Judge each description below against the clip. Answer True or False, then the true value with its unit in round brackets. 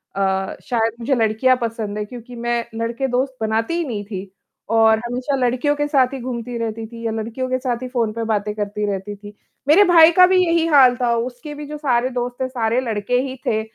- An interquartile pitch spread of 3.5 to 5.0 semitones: False (2.8 semitones)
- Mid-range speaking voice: False (240 Hz)